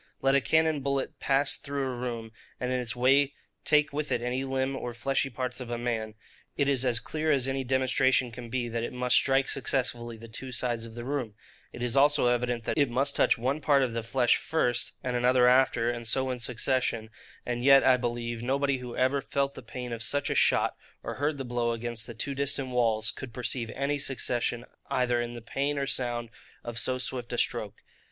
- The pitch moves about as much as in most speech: No, narrow, 2.3 semitones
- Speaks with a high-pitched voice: No, low, 125 Hz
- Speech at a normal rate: No, fast, 220 wpm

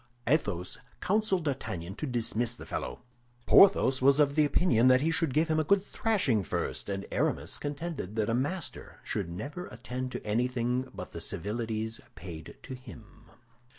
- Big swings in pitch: Yes, wide, 5.7 semitones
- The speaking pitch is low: Yes, low, 130 Hz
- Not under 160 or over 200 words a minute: Yes, average, 165 wpm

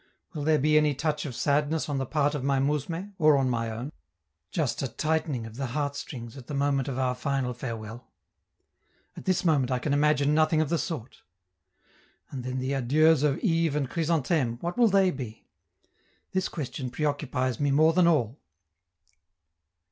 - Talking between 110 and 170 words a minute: No, average, 180 wpm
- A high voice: No, medium, 145 Hz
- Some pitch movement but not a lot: Yes, average, 3.4 semitones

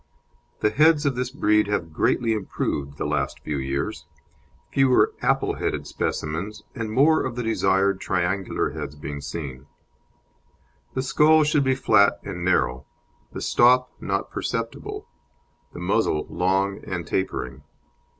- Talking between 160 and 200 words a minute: No, slow, 135 wpm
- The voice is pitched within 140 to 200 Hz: No, low, 100 Hz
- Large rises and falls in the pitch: Yes, wide, 8.9 semitones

